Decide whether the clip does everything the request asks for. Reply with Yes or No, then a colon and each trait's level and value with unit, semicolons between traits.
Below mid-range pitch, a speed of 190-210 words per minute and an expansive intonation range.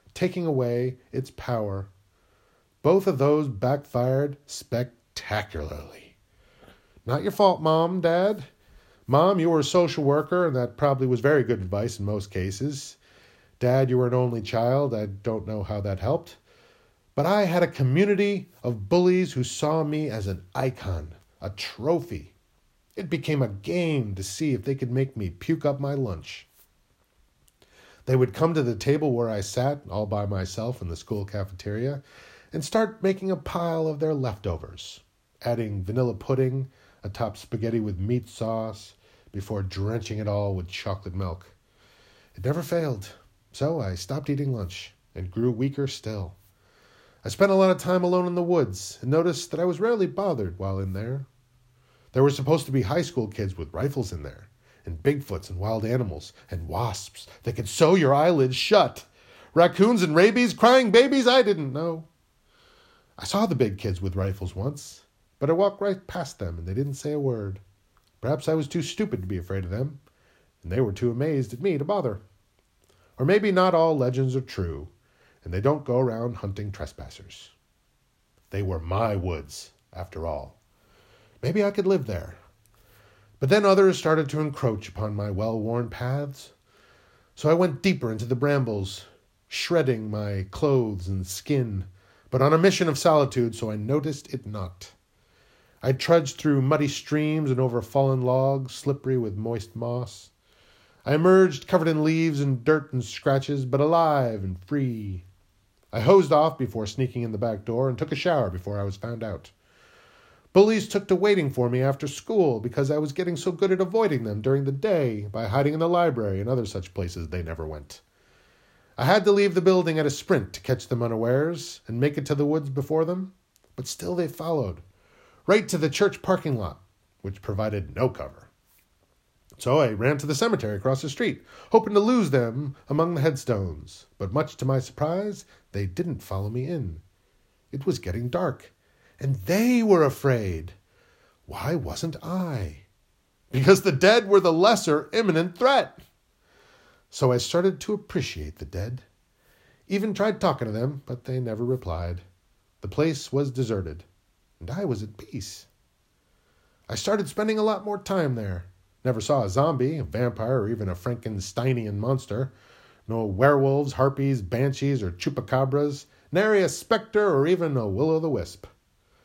No: low, 130 Hz; average, 175 wpm; wide, 7.6 semitones